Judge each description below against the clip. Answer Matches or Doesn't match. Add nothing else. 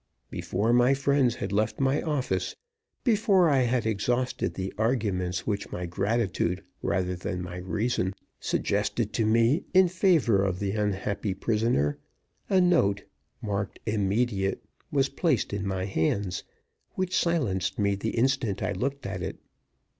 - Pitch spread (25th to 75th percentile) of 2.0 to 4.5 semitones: Doesn't match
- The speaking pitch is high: Doesn't match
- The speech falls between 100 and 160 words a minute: Matches